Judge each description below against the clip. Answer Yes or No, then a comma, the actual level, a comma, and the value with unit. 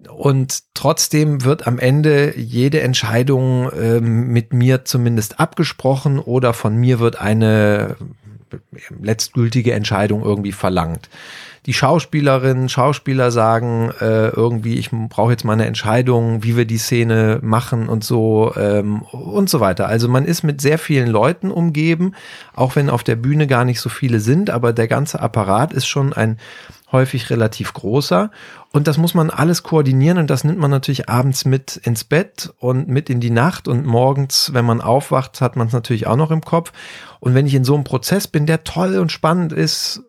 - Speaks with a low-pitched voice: Yes, low, 130 Hz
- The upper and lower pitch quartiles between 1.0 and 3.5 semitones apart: No, average, 4.3 semitones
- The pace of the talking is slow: No, average, 175 wpm